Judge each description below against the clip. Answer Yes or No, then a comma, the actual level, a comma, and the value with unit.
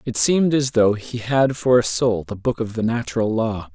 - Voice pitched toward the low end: Yes, low, 115 Hz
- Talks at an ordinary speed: No, fast, 240 wpm